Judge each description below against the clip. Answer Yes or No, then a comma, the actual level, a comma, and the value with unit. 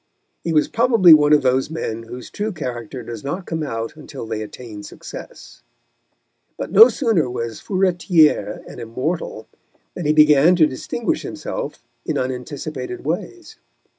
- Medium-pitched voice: Yes, medium, 150 Hz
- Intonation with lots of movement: Yes, wide, 5.9 semitones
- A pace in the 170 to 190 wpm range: No, average, 145 wpm